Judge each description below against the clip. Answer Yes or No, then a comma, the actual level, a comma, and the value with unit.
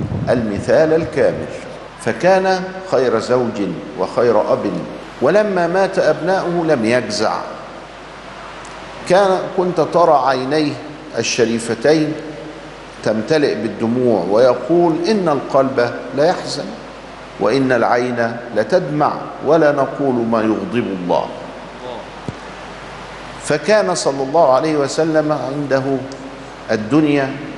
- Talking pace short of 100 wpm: Yes, average, 85 wpm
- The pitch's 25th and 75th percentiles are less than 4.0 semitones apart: No, average, 4.8 semitones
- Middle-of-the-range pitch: Yes, medium, 145 Hz